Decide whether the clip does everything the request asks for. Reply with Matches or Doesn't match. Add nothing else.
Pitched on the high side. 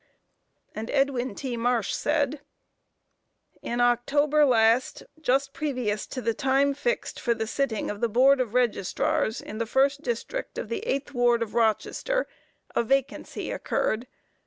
Matches